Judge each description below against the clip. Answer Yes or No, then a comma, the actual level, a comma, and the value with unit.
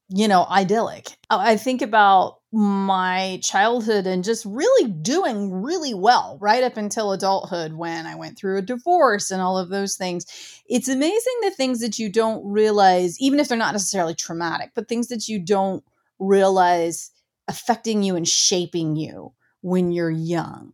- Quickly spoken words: No, average, 165 wpm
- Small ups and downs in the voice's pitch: No, average, 4.1 semitones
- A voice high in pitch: Yes, high, 200 Hz